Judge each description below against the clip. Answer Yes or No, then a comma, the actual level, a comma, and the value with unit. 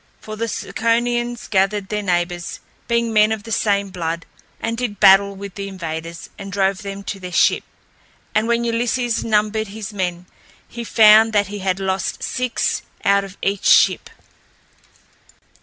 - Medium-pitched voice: No, high, 205 Hz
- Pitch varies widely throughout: No, average, 2.8 semitones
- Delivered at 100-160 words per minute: Yes, average, 155 wpm